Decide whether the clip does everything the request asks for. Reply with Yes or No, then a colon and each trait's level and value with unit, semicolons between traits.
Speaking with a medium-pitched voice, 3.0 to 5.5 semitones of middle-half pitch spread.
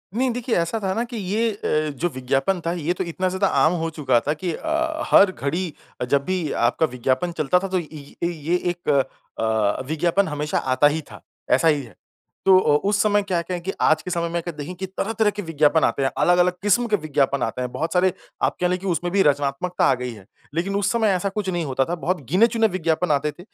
Yes: medium, 175 Hz; average, 4.7 semitones